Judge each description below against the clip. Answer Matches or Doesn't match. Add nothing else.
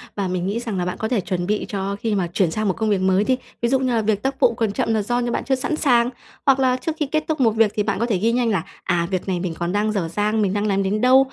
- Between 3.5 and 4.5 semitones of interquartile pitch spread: Matches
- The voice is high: Matches